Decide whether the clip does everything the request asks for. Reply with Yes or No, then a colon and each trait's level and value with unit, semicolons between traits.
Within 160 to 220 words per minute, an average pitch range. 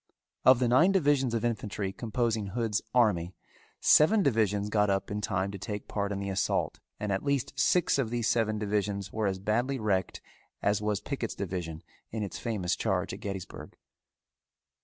Yes: average, 175 wpm; average, 3.2 semitones